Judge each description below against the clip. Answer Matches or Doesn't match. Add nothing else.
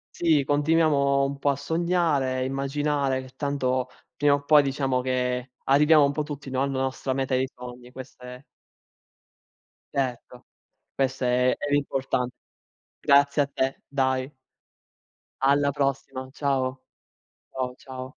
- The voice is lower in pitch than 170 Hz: Matches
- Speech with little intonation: Matches